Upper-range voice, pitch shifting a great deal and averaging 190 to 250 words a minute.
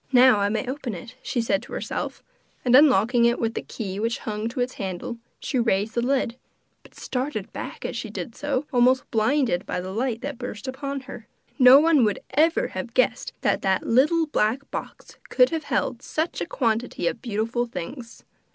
No: high, 245 Hz; average, 3.6 semitones; average, 195 wpm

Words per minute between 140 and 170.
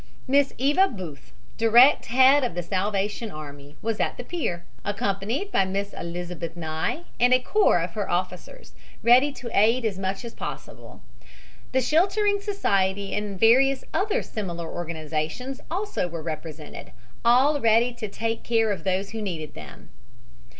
Yes: average, 150 wpm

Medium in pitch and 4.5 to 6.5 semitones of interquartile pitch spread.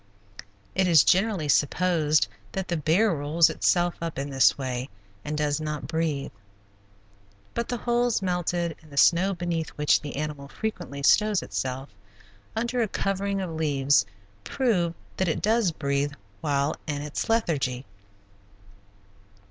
Yes: medium, 160 Hz; average, 4.8 semitones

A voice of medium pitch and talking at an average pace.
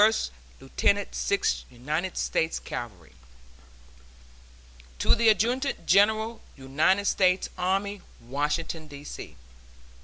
No: medium, 180 Hz; slow, 95 wpm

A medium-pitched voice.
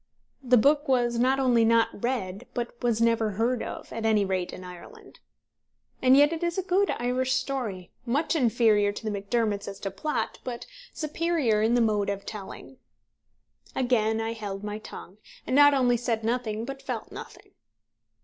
No: high, 235 Hz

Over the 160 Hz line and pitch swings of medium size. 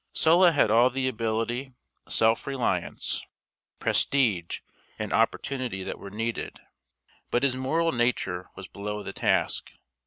No: low, 120 Hz; average, 4.2 semitones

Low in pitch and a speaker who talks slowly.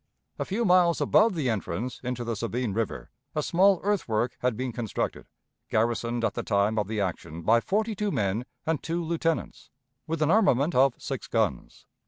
No: low, 125 Hz; average, 180 wpm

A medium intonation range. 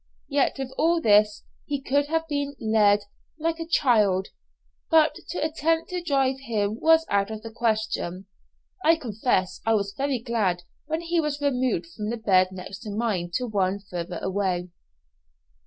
No: wide, 6.3 semitones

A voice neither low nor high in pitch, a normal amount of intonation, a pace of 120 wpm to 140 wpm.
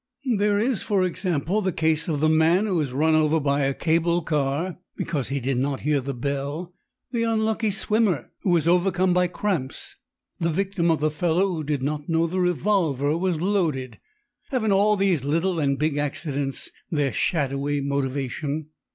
No: medium, 160 Hz; average, 4.5 semitones; average, 175 wpm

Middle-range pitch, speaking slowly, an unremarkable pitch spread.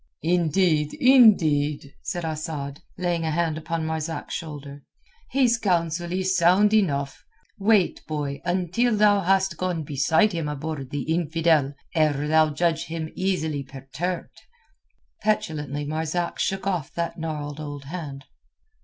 Yes: medium, 160 Hz; slow, 125 wpm; average, 3.6 semitones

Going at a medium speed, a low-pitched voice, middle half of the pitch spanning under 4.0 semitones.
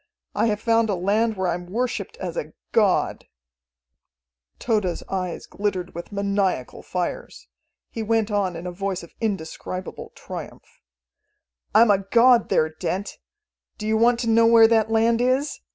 No: average, 155 wpm; high, 210 Hz; average, 3.6 semitones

